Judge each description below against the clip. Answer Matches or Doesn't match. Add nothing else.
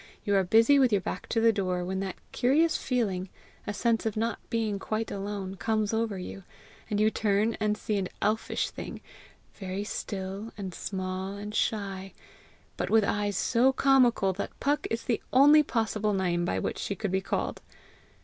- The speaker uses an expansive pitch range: Doesn't match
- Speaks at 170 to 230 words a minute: Matches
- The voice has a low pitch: Doesn't match